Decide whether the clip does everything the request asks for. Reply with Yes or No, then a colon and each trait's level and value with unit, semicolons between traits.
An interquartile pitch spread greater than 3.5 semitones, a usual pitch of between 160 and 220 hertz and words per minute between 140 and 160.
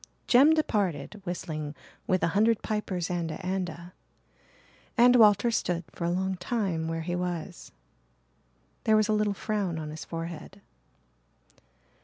Yes: average, 4.0 semitones; medium, 185 Hz; average, 145 wpm